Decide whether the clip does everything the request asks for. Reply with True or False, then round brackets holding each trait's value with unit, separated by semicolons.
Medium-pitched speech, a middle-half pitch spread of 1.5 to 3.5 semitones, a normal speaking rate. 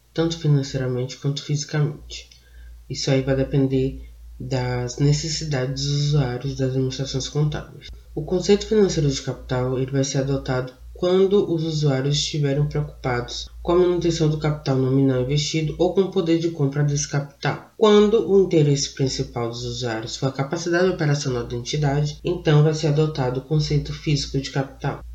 True (145 Hz; 3.0 semitones; 155 wpm)